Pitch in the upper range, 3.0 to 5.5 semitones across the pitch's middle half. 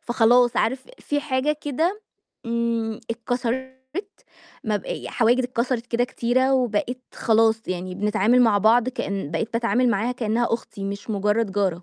No: high, 235 Hz; narrow, 2.6 semitones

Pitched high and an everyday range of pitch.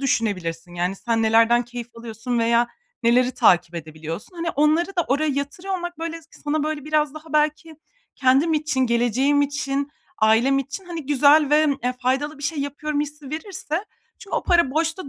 Yes: very high, 285 Hz; average, 4.5 semitones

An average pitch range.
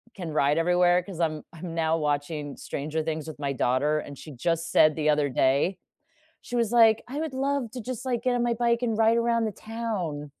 No: wide, 7.4 semitones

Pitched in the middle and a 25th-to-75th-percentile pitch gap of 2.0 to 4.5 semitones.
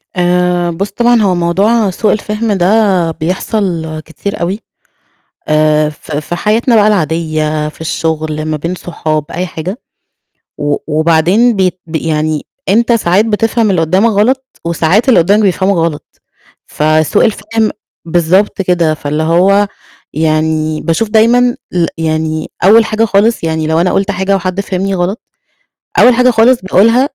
No: medium, 180 Hz; average, 4.9 semitones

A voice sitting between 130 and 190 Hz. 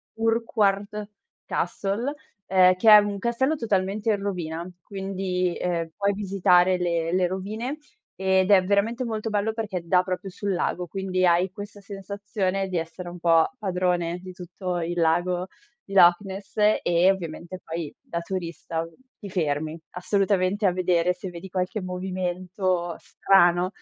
Yes: medium, 185 Hz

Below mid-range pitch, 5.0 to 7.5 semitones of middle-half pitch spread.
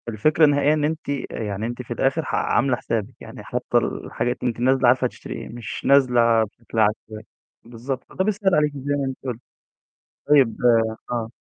No: low, 125 Hz; average, 3.7 semitones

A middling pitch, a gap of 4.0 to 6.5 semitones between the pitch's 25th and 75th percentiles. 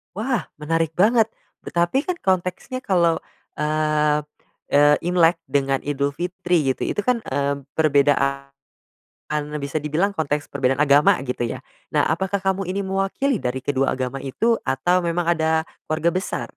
Yes: medium, 160 Hz; average, 5.0 semitones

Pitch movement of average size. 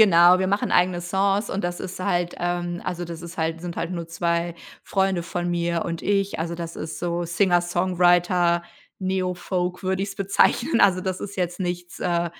No: narrow, 1.5 semitones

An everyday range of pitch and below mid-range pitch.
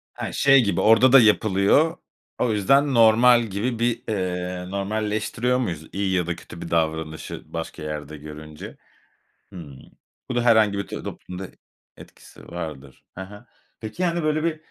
No: wide, 6.0 semitones; low, 100 Hz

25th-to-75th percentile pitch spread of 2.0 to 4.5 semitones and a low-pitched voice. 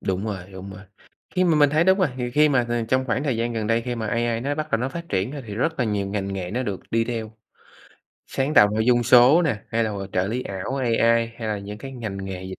Yes: average, 4.1 semitones; low, 115 Hz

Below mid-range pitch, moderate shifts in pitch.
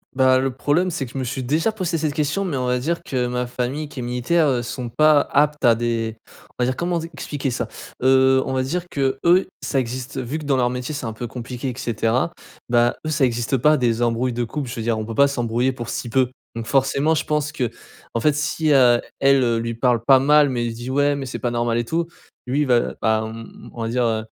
Yes: low, 130 Hz; average, 3.4 semitones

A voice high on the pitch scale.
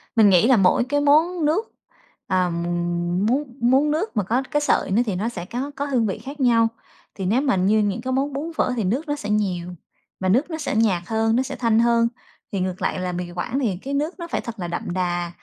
Yes: high, 230 Hz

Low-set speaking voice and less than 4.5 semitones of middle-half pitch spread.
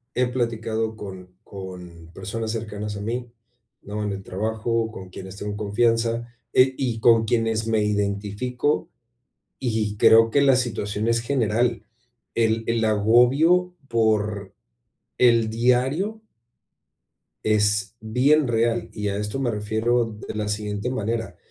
Yes: low, 110 Hz; narrow, 2.4 semitones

